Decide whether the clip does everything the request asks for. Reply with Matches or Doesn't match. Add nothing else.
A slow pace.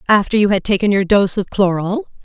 Doesn't match